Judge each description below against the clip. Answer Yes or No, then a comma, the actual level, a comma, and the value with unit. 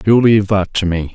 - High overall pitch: No, low, 100 Hz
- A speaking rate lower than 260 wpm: No, fast, 265 wpm